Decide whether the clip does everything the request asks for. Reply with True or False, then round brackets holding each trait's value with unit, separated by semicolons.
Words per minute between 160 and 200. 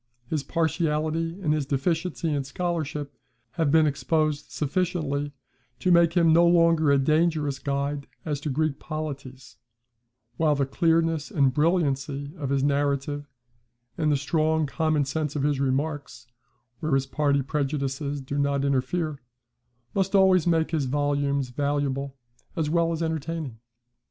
False (140 wpm)